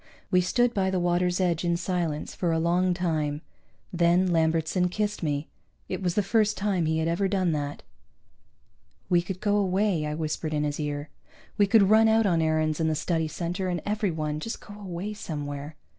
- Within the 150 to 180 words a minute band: No, average, 190 wpm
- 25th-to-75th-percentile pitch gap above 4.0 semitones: No, average, 3.4 semitones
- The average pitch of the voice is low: No, medium, 175 Hz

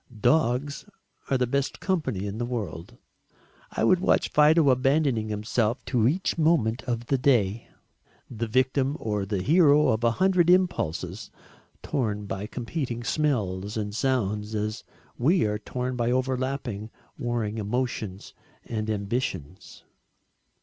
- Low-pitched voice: Yes, low, 120 Hz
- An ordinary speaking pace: No, slow, 130 wpm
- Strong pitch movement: No, average, 4.5 semitones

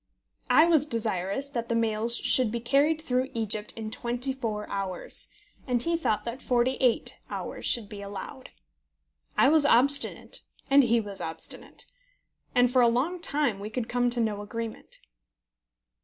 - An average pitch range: Yes, average, 3.5 semitones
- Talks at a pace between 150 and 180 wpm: Yes, average, 160 wpm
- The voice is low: No, high, 235 Hz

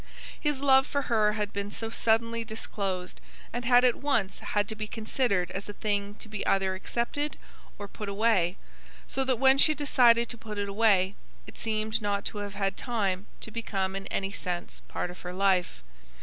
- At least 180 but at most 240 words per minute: Yes, average, 190 wpm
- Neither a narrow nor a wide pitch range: Yes, average, 3.1 semitones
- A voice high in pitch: Yes, high, 210 Hz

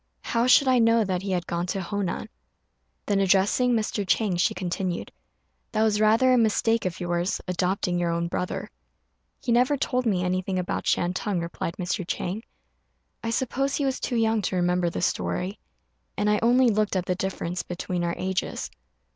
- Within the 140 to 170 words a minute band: No, average, 180 wpm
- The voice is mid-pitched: No, high, 195 Hz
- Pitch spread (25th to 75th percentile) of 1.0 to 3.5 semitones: No, average, 4.1 semitones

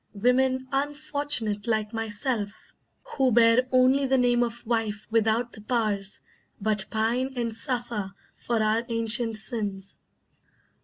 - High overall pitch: Yes, high, 230 Hz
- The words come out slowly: Yes, slow, 120 wpm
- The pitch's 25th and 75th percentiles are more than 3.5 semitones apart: No, average, 2.8 semitones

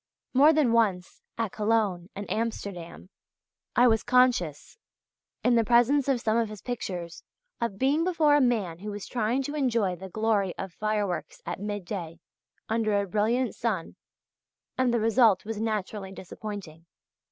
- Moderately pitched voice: No, high, 215 Hz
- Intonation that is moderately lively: Yes, average, 4.0 semitones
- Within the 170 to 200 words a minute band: No, average, 150 wpm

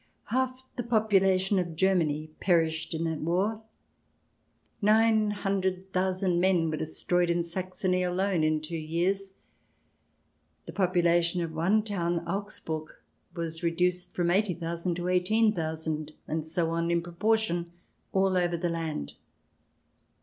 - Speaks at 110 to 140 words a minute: Yes, slow, 135 wpm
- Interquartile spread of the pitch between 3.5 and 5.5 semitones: No, narrow, 2.6 semitones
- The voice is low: No, medium, 175 Hz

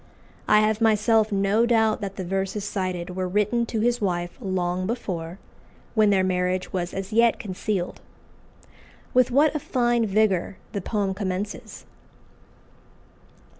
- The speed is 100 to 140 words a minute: Yes, slow, 135 wpm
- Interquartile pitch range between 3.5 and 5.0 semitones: No, average, 3.1 semitones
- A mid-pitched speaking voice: No, high, 200 Hz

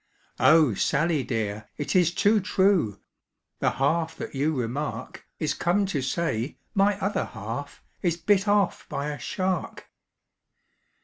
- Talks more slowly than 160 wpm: Yes, slow, 135 wpm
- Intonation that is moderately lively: No, wide, 5.9 semitones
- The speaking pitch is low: No, medium, 160 Hz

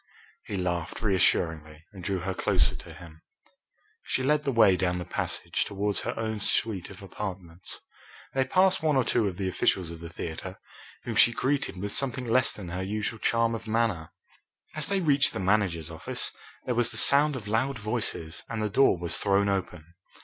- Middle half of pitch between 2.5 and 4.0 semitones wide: No, average, 4.9 semitones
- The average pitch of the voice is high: No, low, 100 Hz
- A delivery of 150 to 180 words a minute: No, average, 190 wpm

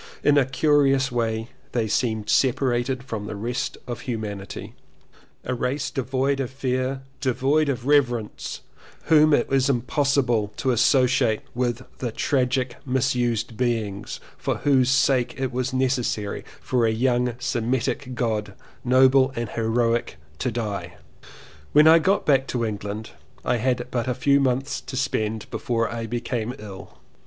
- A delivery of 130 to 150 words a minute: Yes, average, 145 wpm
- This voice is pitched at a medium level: No, low, 125 Hz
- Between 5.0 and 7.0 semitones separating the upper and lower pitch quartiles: No, narrow, 2.5 semitones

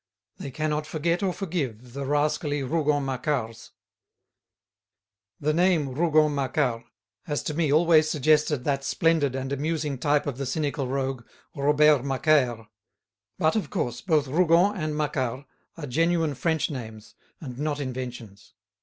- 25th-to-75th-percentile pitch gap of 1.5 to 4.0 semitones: Yes, average, 2.9 semitones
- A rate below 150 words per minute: Yes, slow, 135 wpm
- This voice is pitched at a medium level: Yes, medium, 145 Hz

